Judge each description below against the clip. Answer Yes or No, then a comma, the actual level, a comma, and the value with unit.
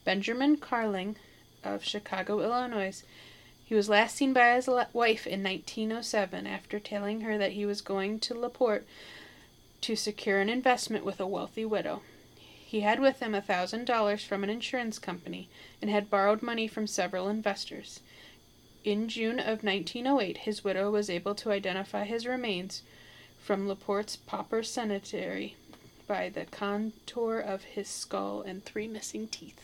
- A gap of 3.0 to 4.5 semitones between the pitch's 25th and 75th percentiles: No, narrow, 2.6 semitones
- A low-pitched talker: No, high, 210 Hz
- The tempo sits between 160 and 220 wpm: No, average, 150 wpm